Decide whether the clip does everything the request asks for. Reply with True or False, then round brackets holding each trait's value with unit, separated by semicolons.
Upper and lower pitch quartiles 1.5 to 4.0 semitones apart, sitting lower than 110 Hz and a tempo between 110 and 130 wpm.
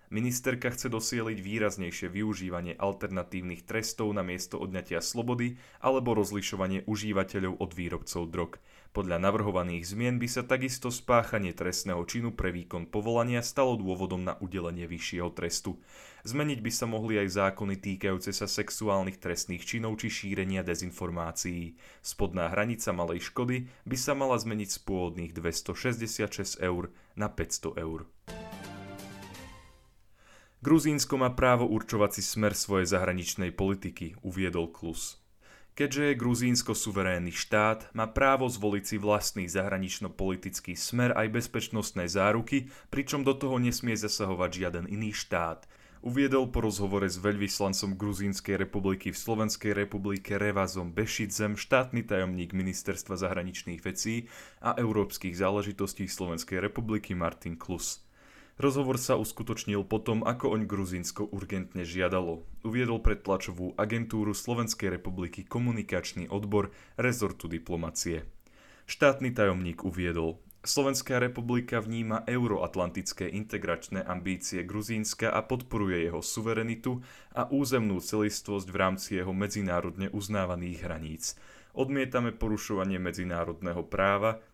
True (3.7 semitones; 100 Hz; 120 wpm)